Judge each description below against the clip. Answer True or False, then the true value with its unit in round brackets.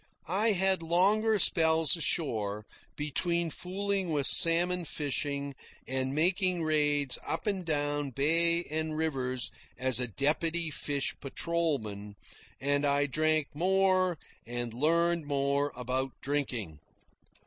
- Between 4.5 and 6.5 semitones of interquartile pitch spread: False (3.8 semitones)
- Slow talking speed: True (115 wpm)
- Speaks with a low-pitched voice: False (155 Hz)